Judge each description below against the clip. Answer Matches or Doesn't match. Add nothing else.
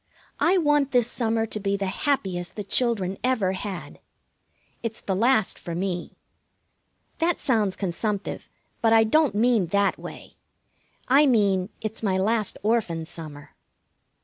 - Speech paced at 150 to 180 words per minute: Doesn't match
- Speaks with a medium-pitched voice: Doesn't match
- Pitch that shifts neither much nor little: Matches